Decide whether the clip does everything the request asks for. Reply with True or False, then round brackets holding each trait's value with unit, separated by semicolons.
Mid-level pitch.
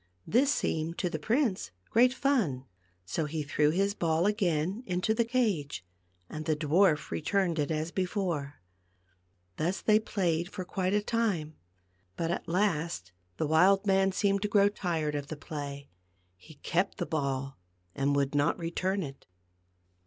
True (170 Hz)